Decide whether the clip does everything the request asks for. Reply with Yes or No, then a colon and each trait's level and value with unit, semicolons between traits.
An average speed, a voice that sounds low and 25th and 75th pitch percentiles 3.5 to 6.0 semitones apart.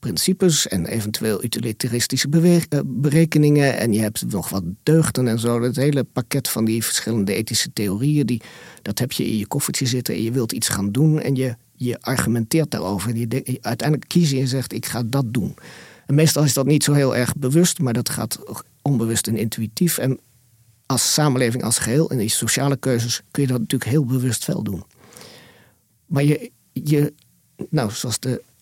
Yes: average, 190 wpm; low, 125 Hz; average, 4.0 semitones